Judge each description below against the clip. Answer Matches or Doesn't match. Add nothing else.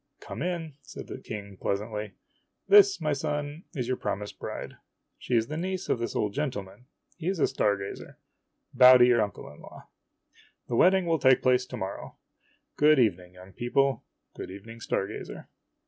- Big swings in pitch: Matches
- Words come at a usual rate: Matches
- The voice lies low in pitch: Matches